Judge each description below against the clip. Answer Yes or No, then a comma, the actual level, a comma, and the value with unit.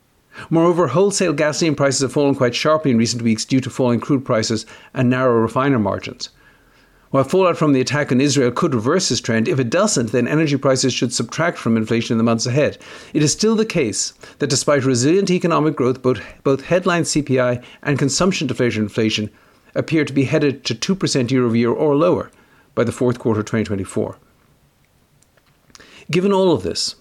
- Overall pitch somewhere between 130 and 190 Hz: Yes, low, 135 Hz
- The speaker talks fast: No, average, 185 wpm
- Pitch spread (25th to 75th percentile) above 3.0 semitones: Yes, average, 4.3 semitones